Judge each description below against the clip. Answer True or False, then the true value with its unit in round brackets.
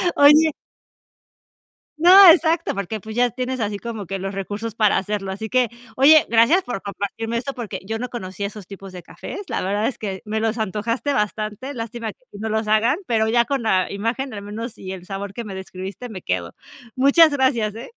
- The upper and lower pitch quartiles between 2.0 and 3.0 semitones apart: False (3.8 semitones)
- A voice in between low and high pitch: False (220 Hz)